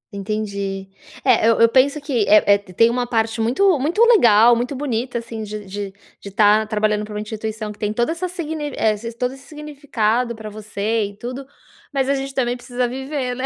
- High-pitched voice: Yes, high, 230 Hz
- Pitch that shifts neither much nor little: Yes, average, 3.9 semitones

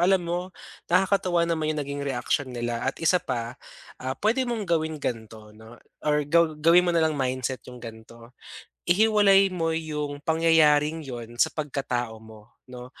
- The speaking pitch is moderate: Yes, medium, 150 Hz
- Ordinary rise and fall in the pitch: No, wide, 5.7 semitones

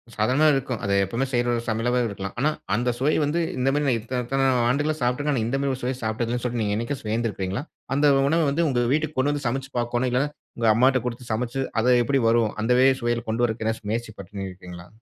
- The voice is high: No, low, 120 Hz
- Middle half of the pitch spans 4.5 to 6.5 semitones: No, average, 3.3 semitones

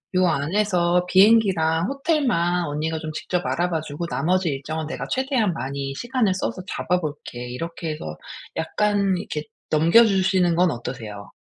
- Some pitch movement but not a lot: Yes, average, 4.1 semitones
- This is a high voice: No, medium, 175 Hz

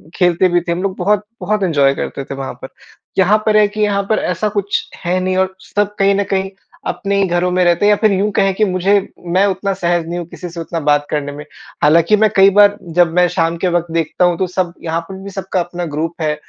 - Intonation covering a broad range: No, average, 2.8 semitones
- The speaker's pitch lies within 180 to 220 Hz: Yes, medium, 185 Hz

